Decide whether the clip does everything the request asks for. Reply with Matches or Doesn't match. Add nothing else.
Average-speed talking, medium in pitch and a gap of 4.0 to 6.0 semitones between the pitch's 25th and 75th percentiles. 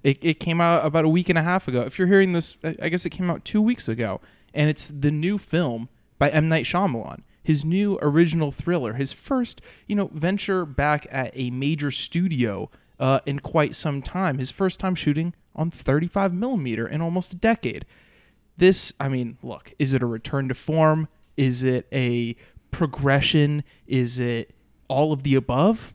Matches